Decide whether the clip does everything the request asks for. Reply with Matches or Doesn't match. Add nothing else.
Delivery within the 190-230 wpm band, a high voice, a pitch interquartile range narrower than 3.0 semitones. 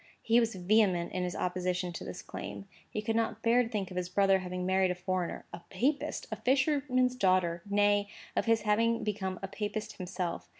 Doesn't match